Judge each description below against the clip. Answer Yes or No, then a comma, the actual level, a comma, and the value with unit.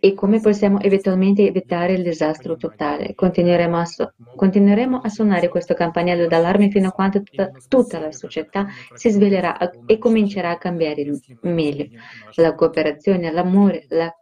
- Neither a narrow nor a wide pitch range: Yes, average, 3.2 semitones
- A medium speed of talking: Yes, average, 150 wpm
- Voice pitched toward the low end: No, medium, 180 Hz